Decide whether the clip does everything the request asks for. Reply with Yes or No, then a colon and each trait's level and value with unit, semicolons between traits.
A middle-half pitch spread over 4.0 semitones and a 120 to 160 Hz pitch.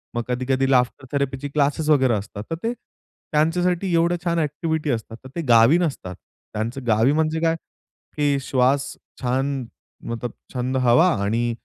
Yes: average, 4.5 semitones; low, 135 Hz